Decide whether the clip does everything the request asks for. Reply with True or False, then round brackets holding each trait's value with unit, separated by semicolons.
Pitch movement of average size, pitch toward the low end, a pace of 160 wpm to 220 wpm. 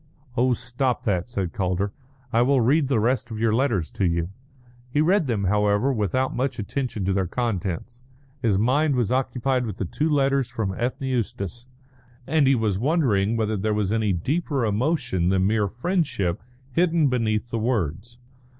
True (4.6 semitones; 115 Hz; 170 wpm)